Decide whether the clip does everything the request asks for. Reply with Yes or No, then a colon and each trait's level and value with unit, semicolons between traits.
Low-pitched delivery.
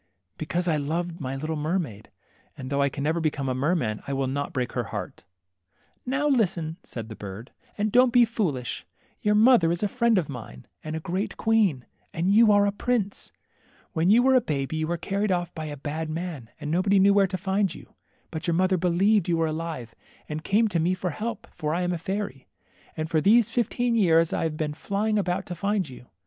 No: medium, 170 Hz